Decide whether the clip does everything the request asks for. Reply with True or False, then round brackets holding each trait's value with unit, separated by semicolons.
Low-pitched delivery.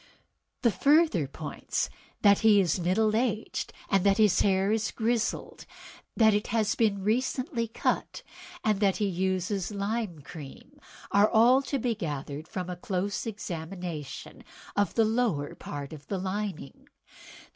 False (200 Hz)